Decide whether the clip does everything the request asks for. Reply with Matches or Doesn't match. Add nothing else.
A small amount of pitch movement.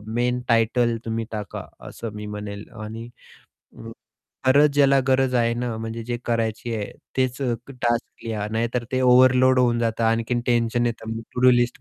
Matches